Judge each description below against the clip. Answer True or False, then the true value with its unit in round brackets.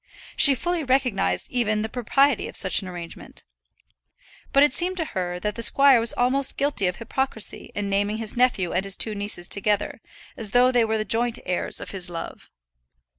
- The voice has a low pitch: False (220 Hz)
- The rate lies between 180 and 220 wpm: True (190 wpm)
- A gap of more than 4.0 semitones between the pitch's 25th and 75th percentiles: True (4.6 semitones)